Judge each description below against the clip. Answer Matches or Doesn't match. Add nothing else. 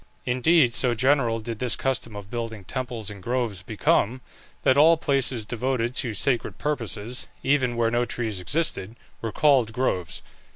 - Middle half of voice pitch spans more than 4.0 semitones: Doesn't match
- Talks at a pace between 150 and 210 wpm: Matches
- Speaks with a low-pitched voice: Matches